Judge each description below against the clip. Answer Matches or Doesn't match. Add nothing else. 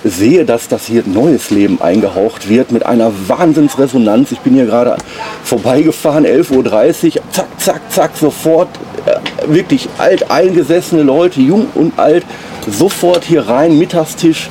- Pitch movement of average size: Doesn't match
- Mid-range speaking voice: Matches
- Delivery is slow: Doesn't match